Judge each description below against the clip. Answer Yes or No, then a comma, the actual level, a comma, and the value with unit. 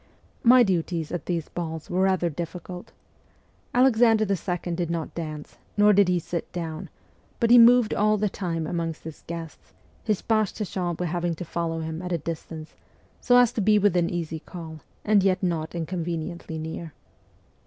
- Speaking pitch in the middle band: Yes, medium, 175 Hz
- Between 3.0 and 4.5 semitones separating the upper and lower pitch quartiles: Yes, average, 3.6 semitones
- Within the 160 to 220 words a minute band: Yes, average, 170 wpm